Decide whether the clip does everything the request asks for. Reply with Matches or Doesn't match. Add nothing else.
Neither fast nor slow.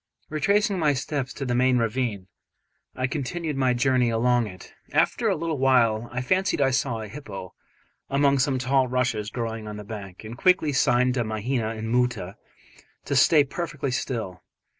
Matches